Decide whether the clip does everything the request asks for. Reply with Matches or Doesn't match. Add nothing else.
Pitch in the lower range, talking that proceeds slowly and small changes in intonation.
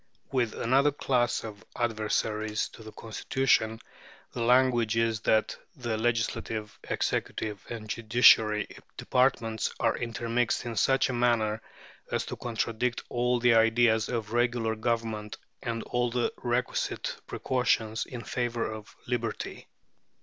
Matches